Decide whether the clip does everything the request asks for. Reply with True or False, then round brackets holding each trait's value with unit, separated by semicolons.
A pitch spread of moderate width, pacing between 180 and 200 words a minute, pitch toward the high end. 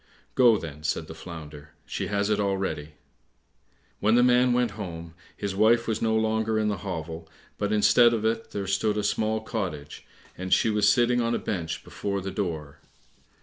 False (4.6 semitones; 185 wpm; 105 Hz)